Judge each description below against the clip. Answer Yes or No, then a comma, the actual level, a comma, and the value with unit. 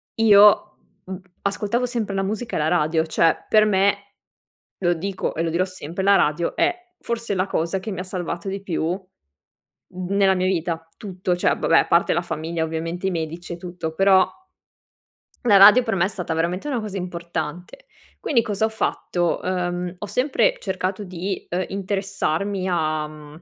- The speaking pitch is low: No, medium, 185 Hz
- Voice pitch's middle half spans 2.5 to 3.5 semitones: Yes, average, 2.8 semitones